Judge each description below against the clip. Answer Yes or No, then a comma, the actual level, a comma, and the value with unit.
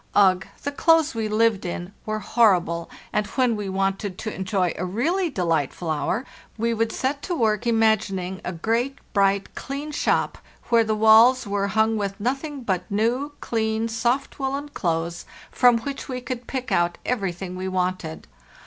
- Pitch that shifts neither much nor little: Yes, average, 4.7 semitones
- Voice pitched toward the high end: Yes, high, 220 Hz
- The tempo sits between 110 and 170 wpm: Yes, average, 165 wpm